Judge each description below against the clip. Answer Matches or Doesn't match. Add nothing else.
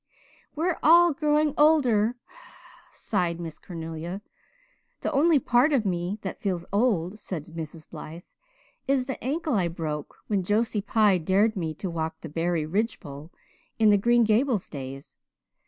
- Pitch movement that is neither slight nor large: Doesn't match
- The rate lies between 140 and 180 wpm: Matches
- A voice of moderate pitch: Doesn't match